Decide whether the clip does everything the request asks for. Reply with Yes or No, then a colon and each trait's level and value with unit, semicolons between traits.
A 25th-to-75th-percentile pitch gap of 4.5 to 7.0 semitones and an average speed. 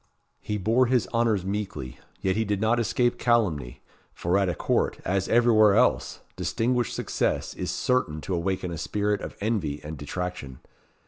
Yes: average, 4.9 semitones; average, 165 wpm